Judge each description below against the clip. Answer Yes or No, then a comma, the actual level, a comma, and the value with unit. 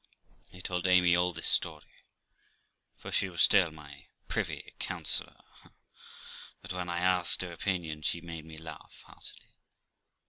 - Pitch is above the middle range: No, very low, 85 Hz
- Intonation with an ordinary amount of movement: No, narrow, 2.0 semitones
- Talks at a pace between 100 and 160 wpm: Yes, average, 140 wpm